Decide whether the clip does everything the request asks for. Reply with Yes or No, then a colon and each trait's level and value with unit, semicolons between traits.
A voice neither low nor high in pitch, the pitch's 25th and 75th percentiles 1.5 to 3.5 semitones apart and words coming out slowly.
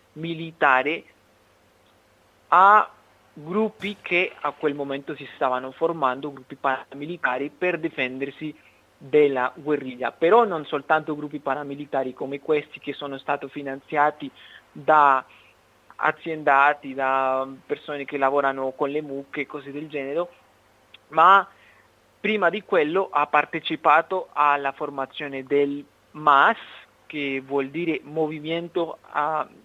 Yes: medium, 145 Hz; average, 2.8 semitones; slow, 110 wpm